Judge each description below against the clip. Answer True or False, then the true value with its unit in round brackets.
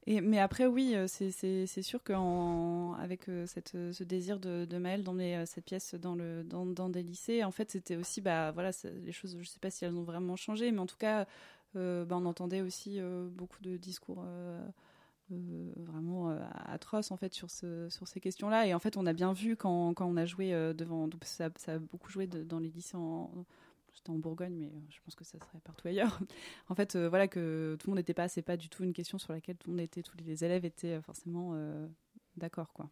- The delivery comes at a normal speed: False (240 wpm)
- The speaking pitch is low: False (180 Hz)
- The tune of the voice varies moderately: False (2.1 semitones)